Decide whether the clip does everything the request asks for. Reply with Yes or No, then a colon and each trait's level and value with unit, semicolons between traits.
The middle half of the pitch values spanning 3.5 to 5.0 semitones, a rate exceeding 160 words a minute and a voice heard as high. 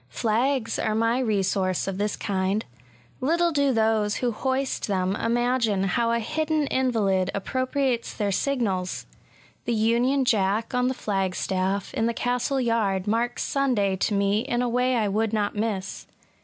No: average, 4.0 semitones; average, 155 wpm; high, 225 Hz